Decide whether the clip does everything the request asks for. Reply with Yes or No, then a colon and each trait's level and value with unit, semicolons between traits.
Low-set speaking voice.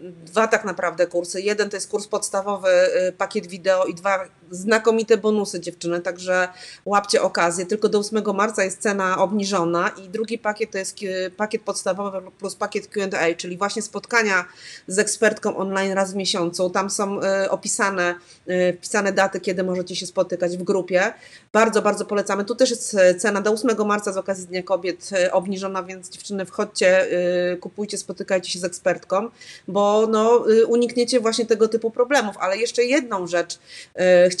No: high, 195 Hz